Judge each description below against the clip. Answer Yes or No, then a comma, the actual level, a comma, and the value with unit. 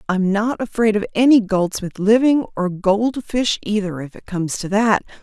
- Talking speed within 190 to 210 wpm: No, average, 160 wpm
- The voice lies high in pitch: Yes, high, 210 Hz